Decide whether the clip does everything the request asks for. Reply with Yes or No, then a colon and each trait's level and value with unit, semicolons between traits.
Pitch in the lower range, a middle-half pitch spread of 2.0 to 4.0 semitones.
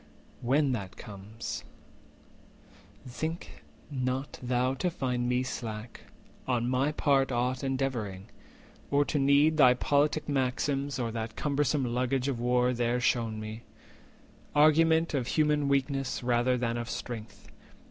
Yes: low, 130 Hz; average, 2.9 semitones